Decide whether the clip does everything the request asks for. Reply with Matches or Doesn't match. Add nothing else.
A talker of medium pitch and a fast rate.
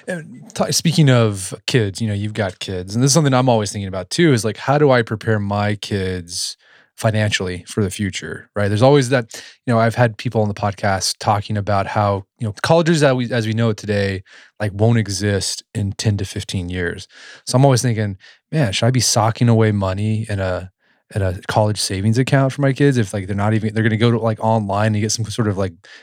Doesn't match